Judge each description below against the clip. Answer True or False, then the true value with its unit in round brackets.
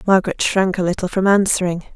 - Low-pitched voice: False (185 Hz)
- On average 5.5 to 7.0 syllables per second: True (6.3 syllables/s)